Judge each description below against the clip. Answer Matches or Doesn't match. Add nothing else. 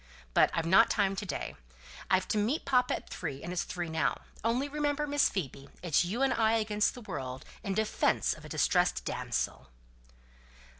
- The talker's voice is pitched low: Doesn't match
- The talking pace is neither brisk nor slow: Matches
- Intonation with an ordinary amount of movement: Doesn't match